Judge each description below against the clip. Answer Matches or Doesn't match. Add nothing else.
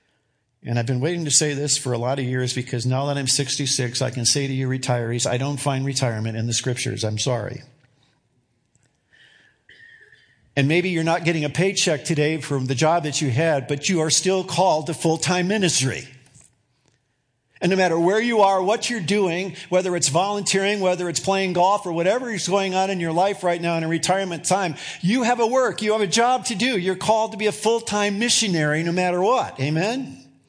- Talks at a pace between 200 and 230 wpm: Matches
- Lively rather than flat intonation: Matches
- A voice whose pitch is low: Doesn't match